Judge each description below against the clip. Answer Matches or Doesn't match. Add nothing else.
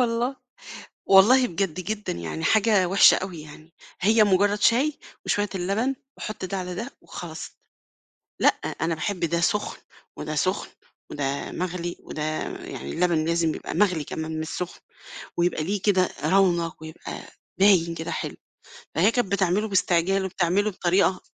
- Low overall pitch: Doesn't match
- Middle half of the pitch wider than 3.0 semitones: Matches